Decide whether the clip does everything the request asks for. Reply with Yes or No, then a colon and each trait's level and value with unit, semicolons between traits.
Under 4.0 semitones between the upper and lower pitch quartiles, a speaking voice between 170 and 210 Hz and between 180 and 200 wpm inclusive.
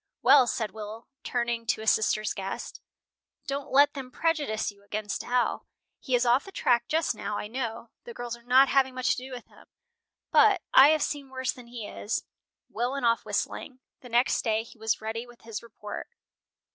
No: average, 3.0 semitones; high, 240 Hz; average, 195 wpm